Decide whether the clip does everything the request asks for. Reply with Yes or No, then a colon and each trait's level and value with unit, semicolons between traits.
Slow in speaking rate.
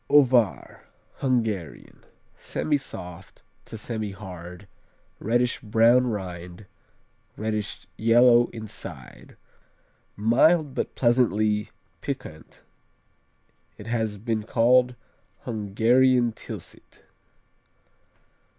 Yes: slow, 70 wpm